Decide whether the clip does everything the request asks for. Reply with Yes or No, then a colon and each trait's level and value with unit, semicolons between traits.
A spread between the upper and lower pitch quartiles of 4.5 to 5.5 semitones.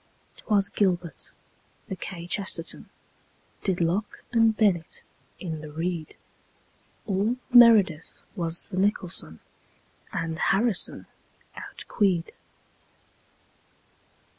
No: average, 3.7 semitones